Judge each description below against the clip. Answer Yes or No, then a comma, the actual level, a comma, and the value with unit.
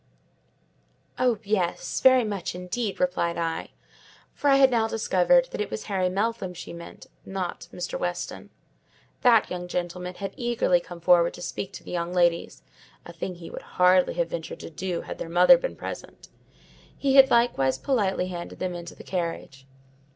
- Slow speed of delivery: No, average, 170 wpm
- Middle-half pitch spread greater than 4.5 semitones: No, average, 4.1 semitones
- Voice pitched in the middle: Yes, medium, 180 Hz